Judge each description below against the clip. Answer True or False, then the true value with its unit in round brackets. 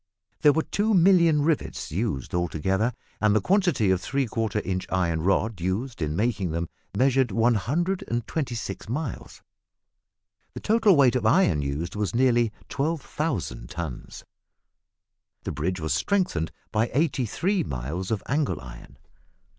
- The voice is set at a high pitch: False (115 Hz)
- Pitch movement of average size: False (8.2 semitones)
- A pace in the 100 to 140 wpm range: True (135 wpm)